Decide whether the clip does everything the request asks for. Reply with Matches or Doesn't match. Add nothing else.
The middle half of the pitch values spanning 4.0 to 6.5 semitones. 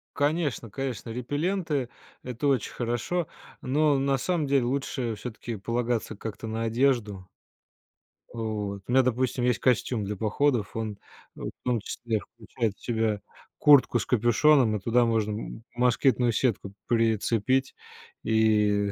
Doesn't match